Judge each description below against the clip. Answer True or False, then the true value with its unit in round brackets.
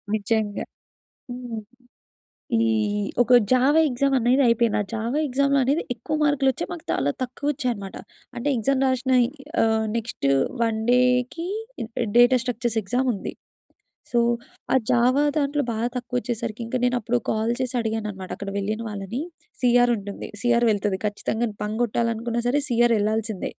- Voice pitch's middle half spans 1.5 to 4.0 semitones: True (2.7 semitones)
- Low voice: False (235 Hz)